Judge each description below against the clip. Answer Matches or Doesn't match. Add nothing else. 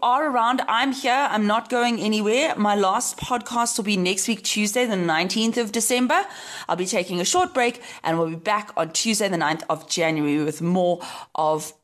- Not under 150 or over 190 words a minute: Doesn't match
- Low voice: Doesn't match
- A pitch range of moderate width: Doesn't match